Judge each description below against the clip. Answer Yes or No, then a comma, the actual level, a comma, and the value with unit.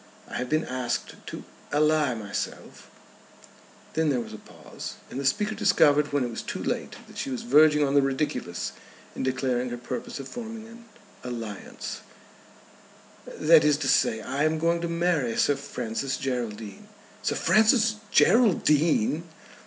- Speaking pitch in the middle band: Yes, medium, 145 Hz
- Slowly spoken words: No, average, 160 wpm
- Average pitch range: Yes, average, 4.6 semitones